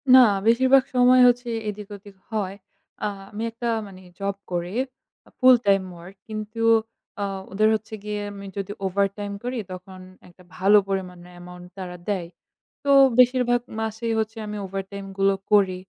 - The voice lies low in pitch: No, high, 200 Hz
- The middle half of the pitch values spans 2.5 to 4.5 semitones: Yes, average, 2.9 semitones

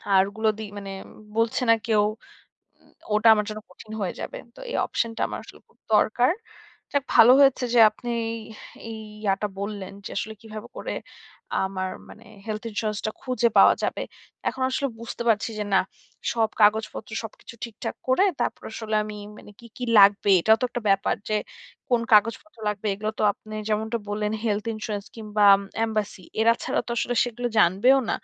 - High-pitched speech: Yes, high, 215 Hz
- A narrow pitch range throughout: Yes, narrow, 2.0 semitones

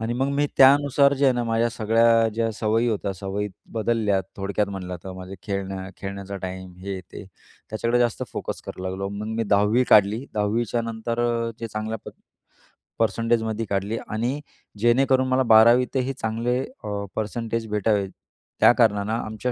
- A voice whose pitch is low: Yes, low, 110 Hz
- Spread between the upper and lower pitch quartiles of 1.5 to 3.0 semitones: Yes, average, 2.7 semitones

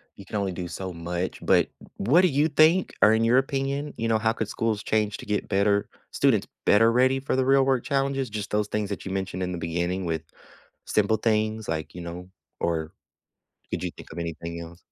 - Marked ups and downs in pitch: Yes, wide, 6.2 semitones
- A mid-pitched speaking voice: No, low, 105 Hz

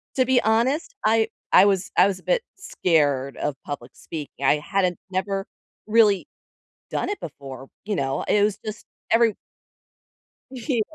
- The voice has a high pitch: Yes, high, 195 Hz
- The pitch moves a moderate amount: No, wide, 7.2 semitones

